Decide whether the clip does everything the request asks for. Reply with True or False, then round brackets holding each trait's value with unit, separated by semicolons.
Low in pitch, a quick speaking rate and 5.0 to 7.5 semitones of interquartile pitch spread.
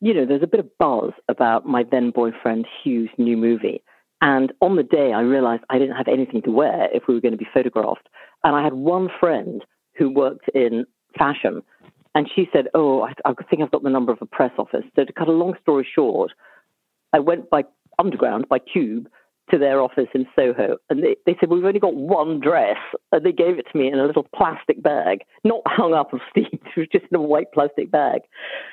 False (145 Hz; 225 wpm; 5.5 semitones)